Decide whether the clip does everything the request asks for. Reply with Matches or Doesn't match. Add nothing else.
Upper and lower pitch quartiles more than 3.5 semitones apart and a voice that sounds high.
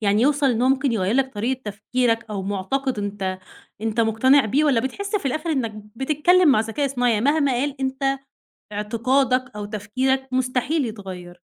Matches